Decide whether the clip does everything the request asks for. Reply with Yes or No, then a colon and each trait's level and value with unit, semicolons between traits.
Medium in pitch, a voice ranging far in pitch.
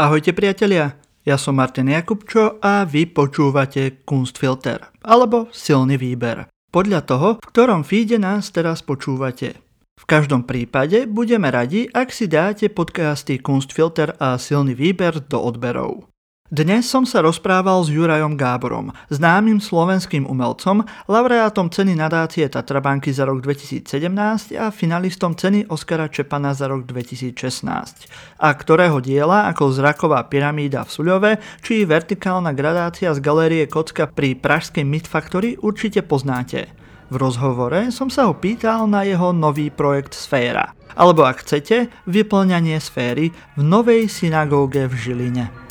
Yes: medium, 155 Hz; wide, 6.2 semitones